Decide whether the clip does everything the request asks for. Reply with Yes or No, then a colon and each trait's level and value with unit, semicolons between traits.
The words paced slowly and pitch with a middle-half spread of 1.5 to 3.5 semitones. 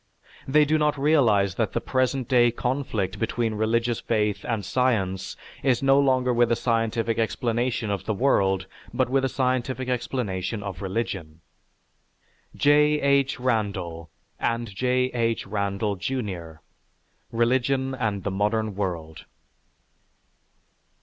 No: slow, 125 wpm; average, 4.3 semitones